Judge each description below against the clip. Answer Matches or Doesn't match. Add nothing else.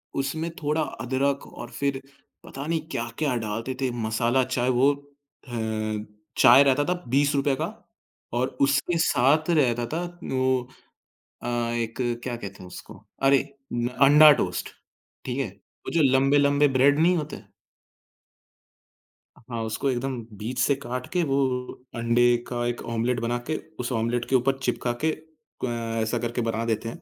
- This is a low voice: Matches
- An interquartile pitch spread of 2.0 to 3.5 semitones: Matches